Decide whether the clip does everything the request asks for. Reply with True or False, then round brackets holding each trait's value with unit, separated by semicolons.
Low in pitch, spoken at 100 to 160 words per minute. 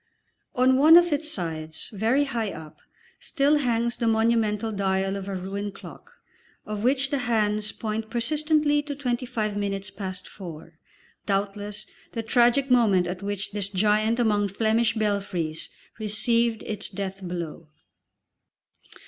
False (215 Hz; 140 wpm)